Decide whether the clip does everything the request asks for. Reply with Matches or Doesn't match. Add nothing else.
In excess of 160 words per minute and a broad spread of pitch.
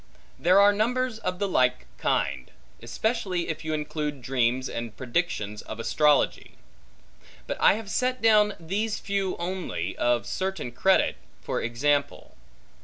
Doesn't match